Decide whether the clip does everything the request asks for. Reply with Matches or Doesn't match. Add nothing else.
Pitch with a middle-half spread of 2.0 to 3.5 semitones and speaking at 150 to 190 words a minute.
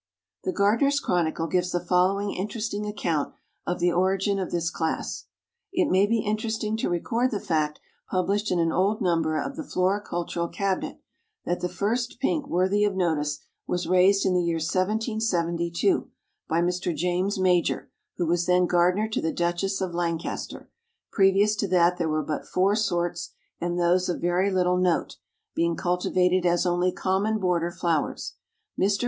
Matches